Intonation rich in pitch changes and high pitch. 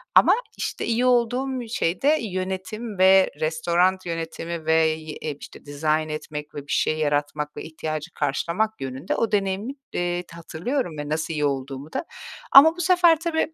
No: wide, 6.5 semitones; medium, 170 Hz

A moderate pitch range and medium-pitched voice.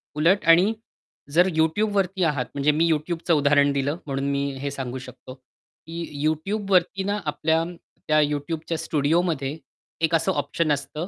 Yes: average, 3.2 semitones; medium, 155 Hz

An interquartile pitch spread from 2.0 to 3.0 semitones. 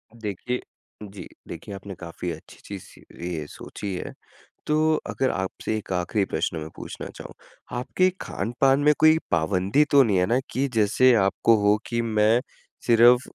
No: average, 4.6 semitones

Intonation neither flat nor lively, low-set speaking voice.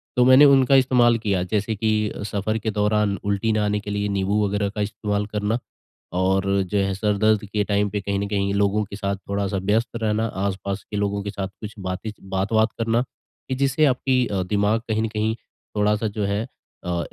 No: narrow, 1.6 semitones; low, 105 Hz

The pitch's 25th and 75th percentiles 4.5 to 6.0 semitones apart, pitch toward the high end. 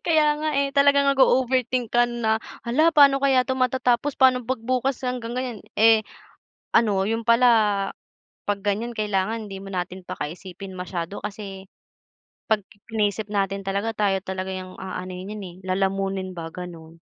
Yes: average, 4.8 semitones; high, 215 Hz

